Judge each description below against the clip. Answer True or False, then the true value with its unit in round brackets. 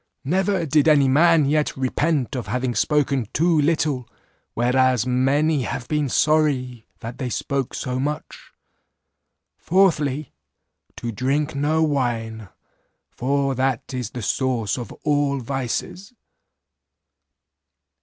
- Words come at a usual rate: False (115 wpm)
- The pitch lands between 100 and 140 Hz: True (135 Hz)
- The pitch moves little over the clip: False (3.1 semitones)